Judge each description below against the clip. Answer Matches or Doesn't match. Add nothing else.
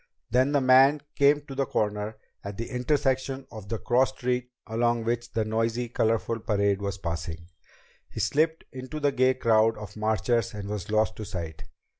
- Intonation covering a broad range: Doesn't match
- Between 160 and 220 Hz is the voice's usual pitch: Doesn't match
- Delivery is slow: Doesn't match